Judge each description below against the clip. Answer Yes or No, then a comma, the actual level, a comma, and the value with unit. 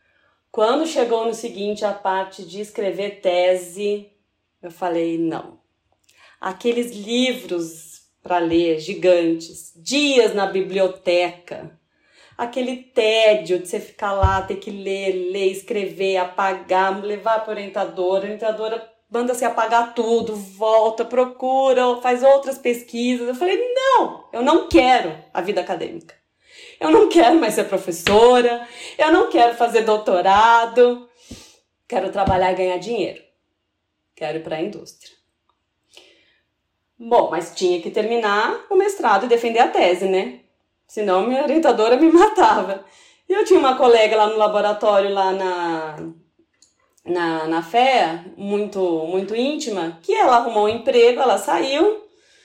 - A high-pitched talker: Yes, high, 215 Hz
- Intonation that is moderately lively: Yes, average, 4.6 semitones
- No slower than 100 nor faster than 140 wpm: Yes, average, 135 wpm